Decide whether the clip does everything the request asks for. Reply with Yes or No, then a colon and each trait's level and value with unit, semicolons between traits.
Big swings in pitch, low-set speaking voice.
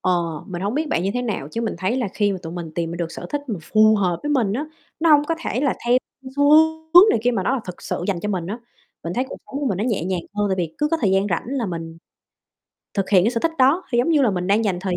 No: wide, 6.1 semitones; high, 210 Hz